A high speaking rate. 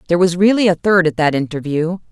Yes: fast, 225 wpm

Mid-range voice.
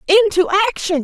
No: very high, 385 Hz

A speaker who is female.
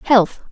Yes: female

